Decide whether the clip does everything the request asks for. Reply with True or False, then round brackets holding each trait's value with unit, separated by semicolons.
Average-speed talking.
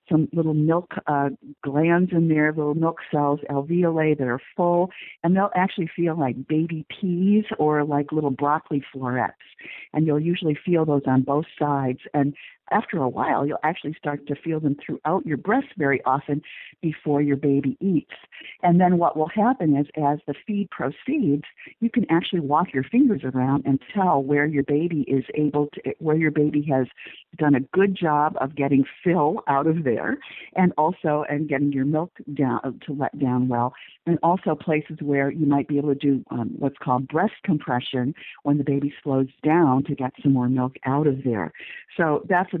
True (190 wpm)